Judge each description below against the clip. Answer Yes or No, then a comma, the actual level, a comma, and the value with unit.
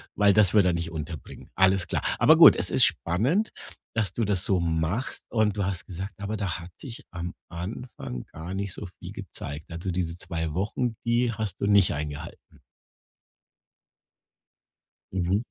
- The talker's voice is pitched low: Yes, very low, 95 Hz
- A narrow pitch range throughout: No, average, 3.7 semitones